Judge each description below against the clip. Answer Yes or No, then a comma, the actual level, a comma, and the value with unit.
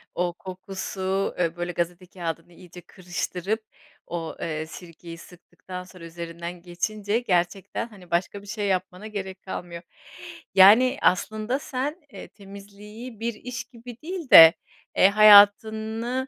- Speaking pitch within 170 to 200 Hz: Yes, high, 190 Hz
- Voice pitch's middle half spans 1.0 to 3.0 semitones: No, average, 3.7 semitones